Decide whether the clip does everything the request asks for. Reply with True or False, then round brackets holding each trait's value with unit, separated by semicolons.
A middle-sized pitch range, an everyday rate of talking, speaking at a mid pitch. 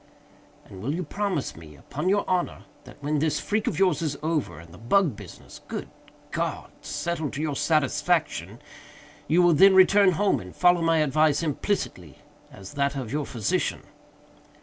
True (4.8 semitones; 170 wpm; 155 Hz)